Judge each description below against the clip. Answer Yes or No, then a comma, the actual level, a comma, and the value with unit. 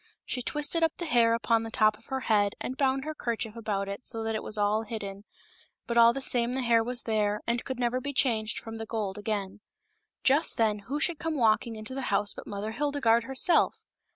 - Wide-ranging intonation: No, average, 3.4 semitones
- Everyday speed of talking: No, fast, 230 wpm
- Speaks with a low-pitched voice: No, high, 230 Hz